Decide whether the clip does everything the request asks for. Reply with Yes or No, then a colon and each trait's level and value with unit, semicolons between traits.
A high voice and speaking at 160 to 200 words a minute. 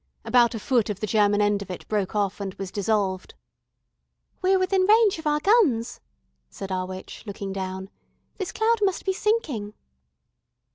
Yes: high, 215 Hz; average, 170 wpm